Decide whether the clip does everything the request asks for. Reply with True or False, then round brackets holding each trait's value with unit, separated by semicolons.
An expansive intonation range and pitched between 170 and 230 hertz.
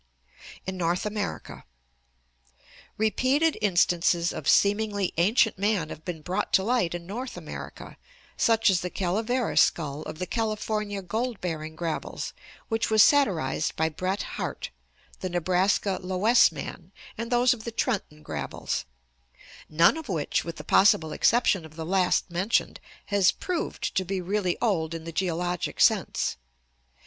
False (4.4 semitones; 190 Hz)